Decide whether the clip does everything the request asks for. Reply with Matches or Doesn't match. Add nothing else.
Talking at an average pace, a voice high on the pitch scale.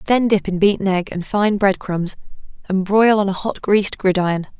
Doesn't match